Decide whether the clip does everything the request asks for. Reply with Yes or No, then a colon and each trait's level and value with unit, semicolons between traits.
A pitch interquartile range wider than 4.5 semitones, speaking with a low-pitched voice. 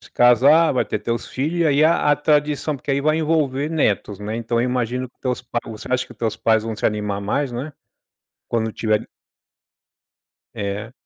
Yes: average, 4.9 semitones; low, 125 Hz